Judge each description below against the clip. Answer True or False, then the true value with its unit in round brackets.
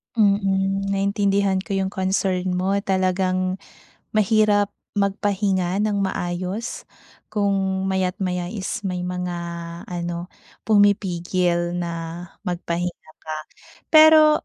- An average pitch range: False (1.9 semitones)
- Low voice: False (190 Hz)